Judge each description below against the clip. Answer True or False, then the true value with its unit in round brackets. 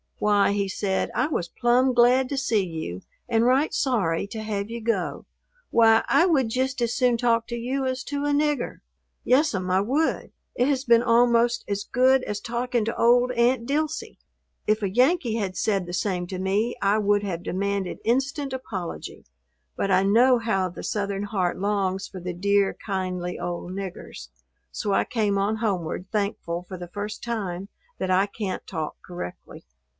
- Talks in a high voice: True (215 Hz)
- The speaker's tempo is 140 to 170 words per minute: False (180 wpm)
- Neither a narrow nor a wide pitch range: True (4.3 semitones)